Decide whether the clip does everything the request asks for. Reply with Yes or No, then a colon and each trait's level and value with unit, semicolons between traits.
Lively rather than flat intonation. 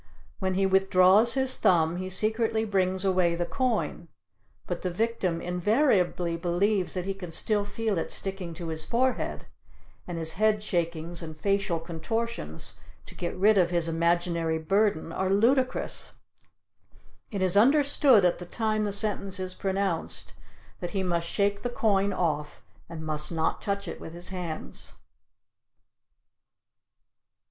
No: average, 3.6 semitones